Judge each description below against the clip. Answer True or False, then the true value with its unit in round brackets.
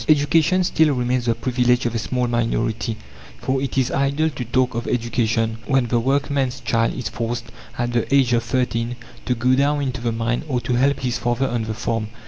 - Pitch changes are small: True (2.3 semitones)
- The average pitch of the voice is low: True (125 Hz)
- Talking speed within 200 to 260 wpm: True (205 wpm)